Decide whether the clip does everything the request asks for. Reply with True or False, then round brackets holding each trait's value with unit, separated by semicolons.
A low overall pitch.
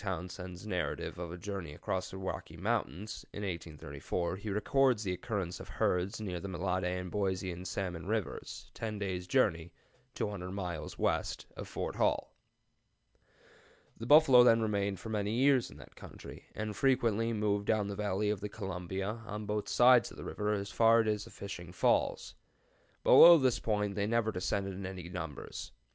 True (100 Hz)